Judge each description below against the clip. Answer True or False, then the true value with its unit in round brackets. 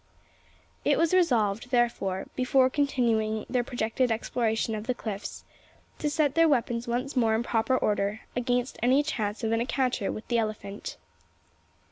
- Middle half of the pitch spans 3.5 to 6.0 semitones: False (2.8 semitones)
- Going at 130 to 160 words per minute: True (150 wpm)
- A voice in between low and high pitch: False (240 Hz)